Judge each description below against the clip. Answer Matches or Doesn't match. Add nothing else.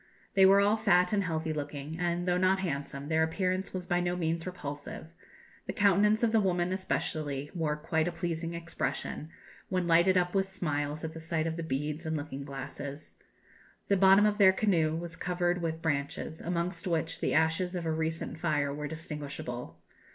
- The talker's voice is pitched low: Doesn't match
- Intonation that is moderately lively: Matches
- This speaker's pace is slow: Doesn't match